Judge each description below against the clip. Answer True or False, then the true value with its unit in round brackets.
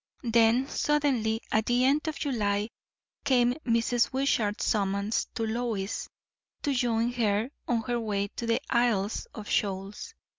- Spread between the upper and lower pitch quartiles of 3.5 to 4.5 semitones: False (2.7 semitones)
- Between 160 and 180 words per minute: False (140 wpm)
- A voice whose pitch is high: True (230 Hz)